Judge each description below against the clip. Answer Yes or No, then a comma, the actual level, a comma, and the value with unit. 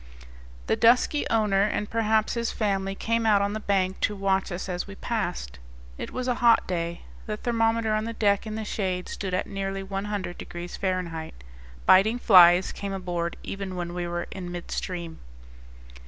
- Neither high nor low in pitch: No, high, 195 Hz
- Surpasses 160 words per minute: Yes, average, 175 wpm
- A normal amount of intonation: Yes, average, 3.3 semitones